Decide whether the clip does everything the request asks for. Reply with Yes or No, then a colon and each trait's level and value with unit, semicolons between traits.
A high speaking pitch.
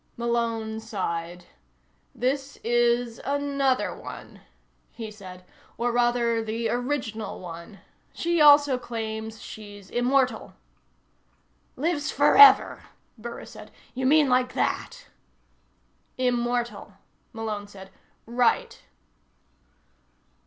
Yes: high, 235 Hz